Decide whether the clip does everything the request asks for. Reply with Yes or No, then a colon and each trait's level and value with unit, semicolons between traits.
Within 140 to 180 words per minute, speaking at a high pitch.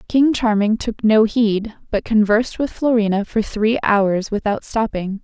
Yes: average, 160 wpm; high, 215 Hz